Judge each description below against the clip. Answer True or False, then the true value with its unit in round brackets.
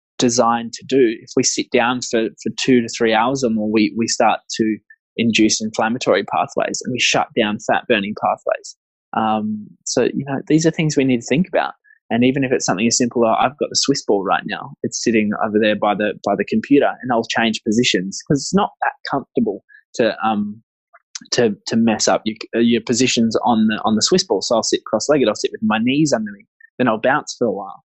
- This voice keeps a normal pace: False (230 wpm)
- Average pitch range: False (5.9 semitones)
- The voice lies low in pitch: True (115 Hz)